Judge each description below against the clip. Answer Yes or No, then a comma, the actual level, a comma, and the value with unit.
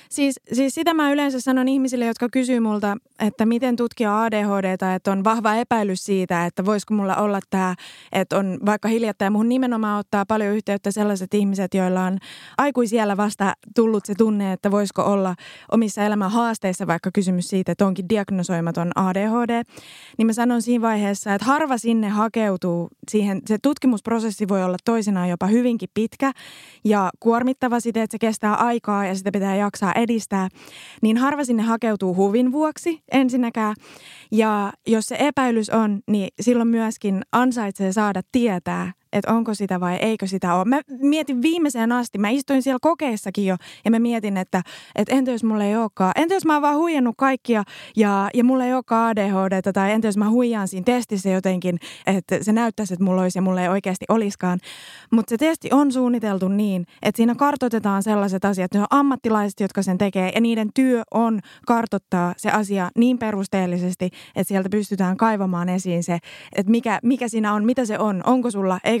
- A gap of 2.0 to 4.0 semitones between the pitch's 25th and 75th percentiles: Yes, average, 3.4 semitones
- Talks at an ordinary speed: No, fast, 180 wpm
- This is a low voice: No, high, 215 Hz